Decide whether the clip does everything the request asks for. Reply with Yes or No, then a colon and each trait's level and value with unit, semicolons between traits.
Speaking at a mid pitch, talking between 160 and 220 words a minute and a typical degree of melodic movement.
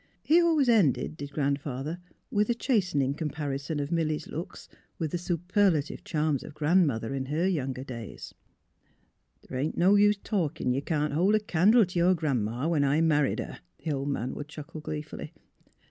Yes: medium, 155 Hz; average, 190 wpm; average, 4.2 semitones